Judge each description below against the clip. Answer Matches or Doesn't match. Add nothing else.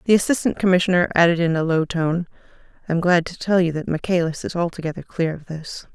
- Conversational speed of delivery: Doesn't match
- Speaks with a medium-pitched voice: Matches